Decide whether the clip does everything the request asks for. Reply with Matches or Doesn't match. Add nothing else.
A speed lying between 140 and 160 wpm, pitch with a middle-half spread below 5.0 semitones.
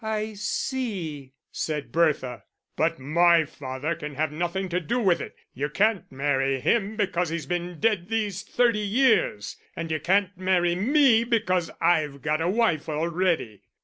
Doesn't match